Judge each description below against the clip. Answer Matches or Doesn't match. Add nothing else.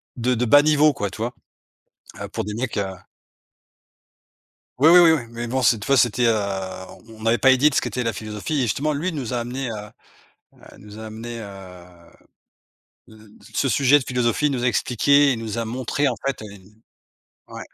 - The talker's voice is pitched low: Matches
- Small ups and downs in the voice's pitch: Doesn't match